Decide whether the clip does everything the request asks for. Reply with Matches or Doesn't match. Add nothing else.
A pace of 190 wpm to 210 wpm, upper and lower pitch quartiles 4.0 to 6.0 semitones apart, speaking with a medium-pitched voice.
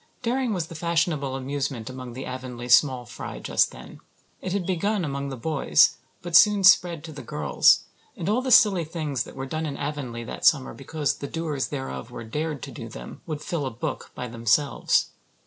Matches